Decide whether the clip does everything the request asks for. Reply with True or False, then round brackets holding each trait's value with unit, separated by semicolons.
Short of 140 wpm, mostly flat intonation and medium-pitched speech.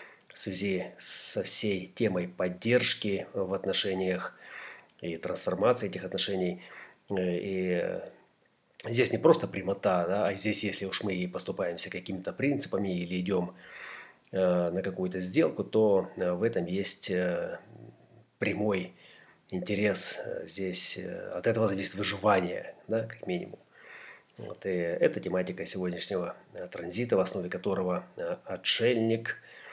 False (115 wpm; 1.7 semitones; 95 Hz)